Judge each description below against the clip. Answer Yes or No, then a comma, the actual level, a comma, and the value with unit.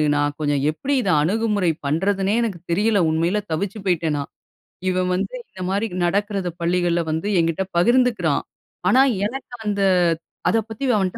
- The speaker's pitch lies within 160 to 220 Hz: Yes, high, 190 Hz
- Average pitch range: Yes, average, 3.8 semitones